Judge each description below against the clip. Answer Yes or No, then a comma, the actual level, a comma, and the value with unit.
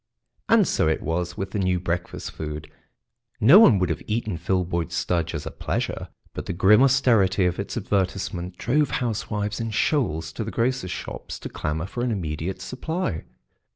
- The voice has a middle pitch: No, very low, 95 Hz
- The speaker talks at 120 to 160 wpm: No, average, 175 wpm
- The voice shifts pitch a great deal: No, average, 5.0 semitones